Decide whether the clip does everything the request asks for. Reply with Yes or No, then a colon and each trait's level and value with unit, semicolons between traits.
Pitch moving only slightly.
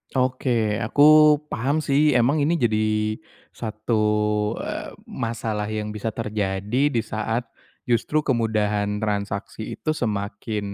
No: average, 3.0 semitones